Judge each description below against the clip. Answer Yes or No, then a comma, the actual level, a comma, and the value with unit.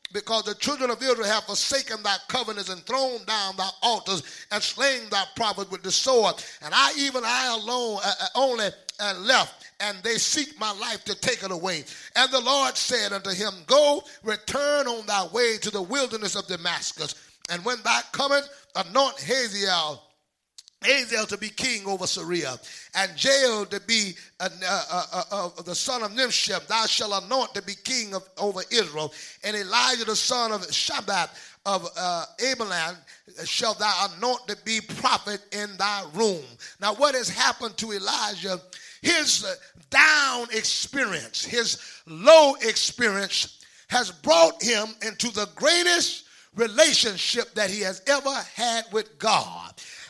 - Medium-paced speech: Yes, average, 160 wpm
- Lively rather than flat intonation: No, average, 4.2 semitones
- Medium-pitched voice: No, high, 215 Hz